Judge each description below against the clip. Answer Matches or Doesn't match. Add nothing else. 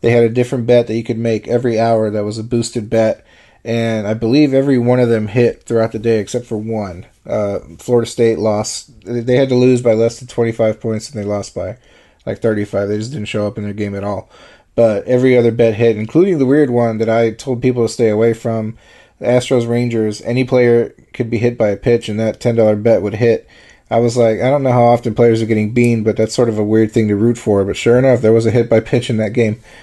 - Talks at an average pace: Doesn't match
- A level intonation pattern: Matches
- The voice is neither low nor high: Doesn't match